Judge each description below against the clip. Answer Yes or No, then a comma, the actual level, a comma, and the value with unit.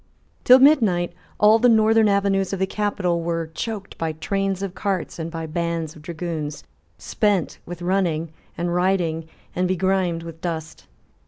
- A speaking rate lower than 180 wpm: Yes, average, 155 wpm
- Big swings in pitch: No, average, 3.0 semitones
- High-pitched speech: No, medium, 180 Hz